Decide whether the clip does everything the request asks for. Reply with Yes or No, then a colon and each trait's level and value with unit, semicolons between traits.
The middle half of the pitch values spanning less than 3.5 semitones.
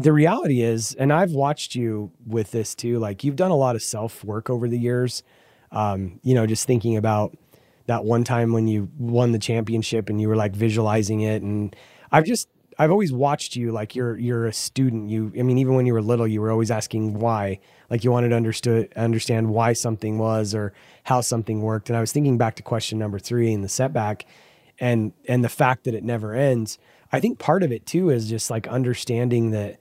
Yes: narrow, 2.4 semitones